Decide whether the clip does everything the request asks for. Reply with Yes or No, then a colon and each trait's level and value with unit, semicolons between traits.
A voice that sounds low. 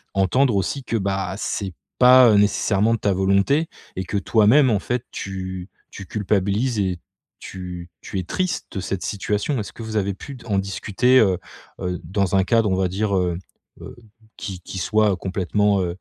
Yes: low, 100 Hz